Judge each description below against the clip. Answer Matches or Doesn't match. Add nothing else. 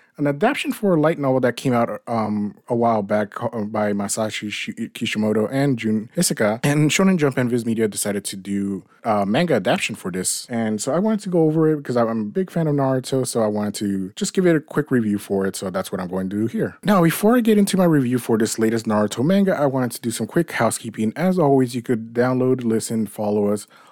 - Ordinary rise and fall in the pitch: Doesn't match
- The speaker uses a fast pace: Matches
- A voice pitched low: Matches